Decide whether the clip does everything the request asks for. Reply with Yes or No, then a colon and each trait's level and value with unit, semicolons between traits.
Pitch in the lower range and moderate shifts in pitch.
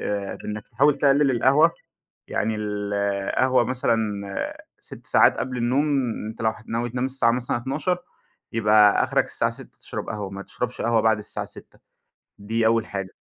Yes: low, 115 Hz; average, 3.6 semitones